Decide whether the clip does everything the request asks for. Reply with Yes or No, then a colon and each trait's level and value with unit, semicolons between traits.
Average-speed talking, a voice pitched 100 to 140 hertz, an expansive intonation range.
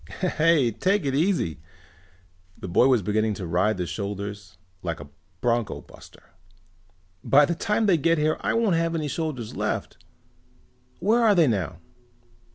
Yes: average, 155 wpm; low, 135 Hz; wide, 8.7 semitones